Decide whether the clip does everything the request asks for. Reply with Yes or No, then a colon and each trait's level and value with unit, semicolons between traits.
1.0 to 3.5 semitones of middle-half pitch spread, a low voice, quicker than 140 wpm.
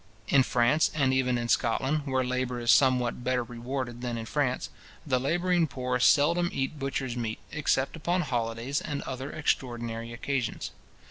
Yes: average, 2.7 semitones; low, 130 Hz; average, 155 wpm